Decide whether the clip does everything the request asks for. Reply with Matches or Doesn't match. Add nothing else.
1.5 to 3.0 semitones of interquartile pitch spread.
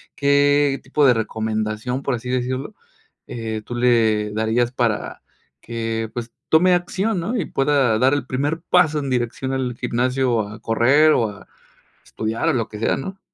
Doesn't match